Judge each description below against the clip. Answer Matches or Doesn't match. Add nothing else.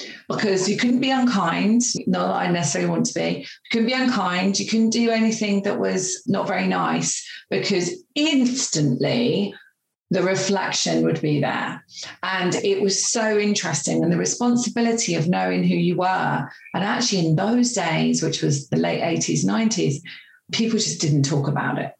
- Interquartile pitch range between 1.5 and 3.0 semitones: Doesn't match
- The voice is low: Doesn't match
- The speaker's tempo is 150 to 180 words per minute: Matches